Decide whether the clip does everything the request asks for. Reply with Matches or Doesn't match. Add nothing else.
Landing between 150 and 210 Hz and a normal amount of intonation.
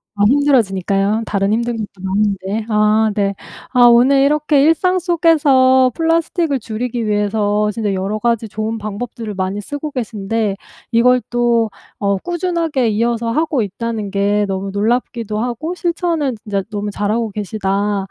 Doesn't match